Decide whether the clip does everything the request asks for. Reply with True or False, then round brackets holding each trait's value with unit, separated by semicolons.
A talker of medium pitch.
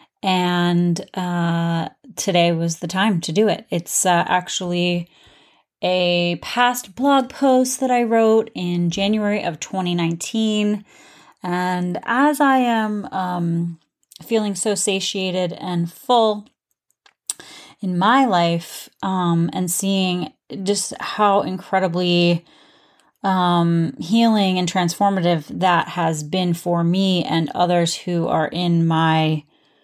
True (180 Hz)